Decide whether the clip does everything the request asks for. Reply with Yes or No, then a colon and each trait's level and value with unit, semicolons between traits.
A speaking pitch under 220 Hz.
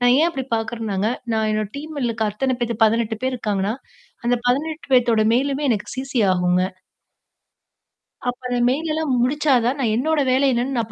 No: high, 245 Hz